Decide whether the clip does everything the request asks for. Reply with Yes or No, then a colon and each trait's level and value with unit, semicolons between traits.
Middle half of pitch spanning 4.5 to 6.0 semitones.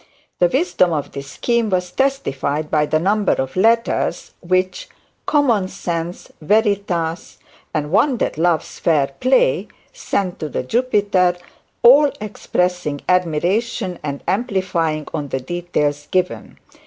Yes: wide, 5.5 semitones